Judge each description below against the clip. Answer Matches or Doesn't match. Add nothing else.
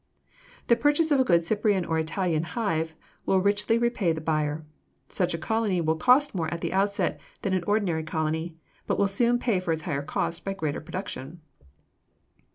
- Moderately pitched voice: Matches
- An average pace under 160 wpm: Doesn't match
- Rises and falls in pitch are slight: Doesn't match